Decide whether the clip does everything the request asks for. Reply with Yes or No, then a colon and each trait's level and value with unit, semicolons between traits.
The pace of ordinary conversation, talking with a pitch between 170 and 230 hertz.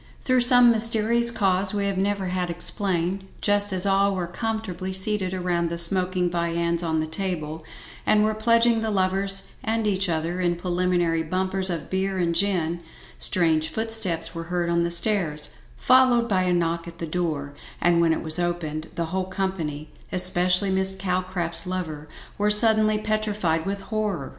Yes: average, 165 wpm; medium, 185 Hz